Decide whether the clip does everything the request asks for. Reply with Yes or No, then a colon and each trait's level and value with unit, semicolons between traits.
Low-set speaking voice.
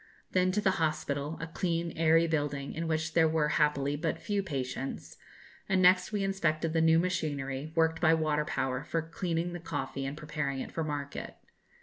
No: medium, 160 Hz